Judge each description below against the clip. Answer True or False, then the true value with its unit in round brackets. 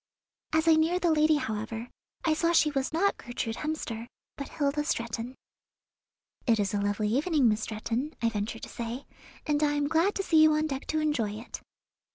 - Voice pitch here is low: False (280 Hz)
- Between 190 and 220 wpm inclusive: True (195 wpm)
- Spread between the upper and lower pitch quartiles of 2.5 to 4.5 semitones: False (5.5 semitones)